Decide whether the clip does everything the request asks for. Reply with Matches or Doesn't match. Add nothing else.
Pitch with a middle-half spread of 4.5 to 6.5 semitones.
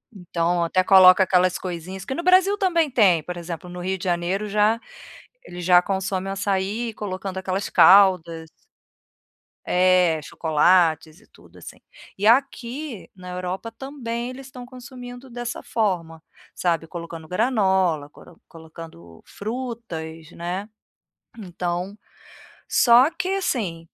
Matches